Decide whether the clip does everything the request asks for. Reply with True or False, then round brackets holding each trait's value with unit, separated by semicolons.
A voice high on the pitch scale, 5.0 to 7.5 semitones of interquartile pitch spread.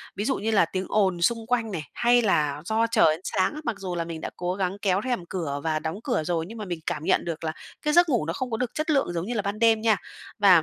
True (195 Hz; 5.3 semitones)